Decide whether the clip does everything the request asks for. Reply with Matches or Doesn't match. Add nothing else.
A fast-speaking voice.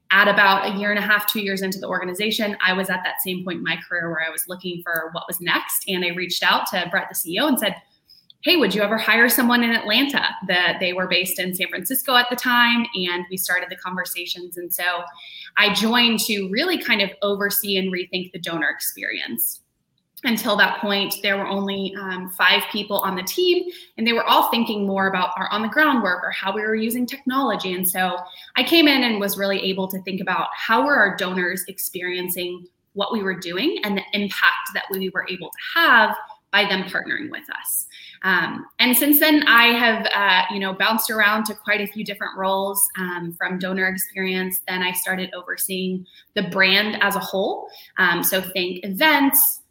Matches